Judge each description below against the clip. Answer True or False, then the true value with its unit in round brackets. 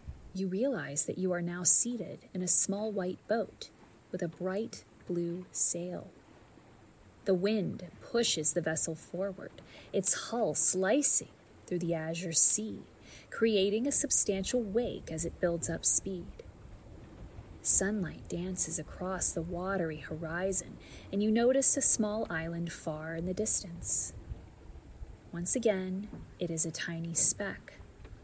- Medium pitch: True (180 Hz)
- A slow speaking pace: True (130 wpm)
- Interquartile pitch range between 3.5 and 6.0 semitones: True (3.8 semitones)